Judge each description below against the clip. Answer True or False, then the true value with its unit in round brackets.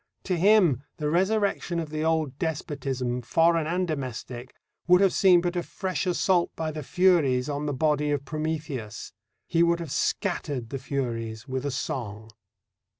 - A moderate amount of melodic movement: True (4.7 semitones)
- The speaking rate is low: False (160 wpm)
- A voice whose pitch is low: False (155 Hz)